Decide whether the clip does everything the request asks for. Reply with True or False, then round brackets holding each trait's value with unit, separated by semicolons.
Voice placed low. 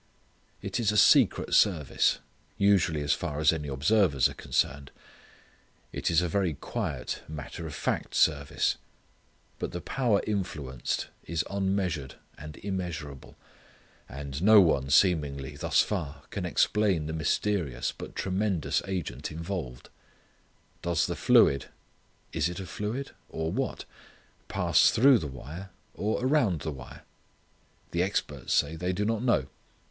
True (85 Hz)